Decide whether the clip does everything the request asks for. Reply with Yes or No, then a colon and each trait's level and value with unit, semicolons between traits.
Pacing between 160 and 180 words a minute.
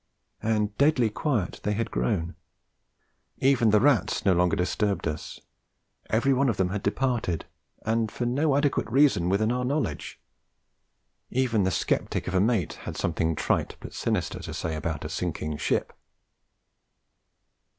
No: average, 150 wpm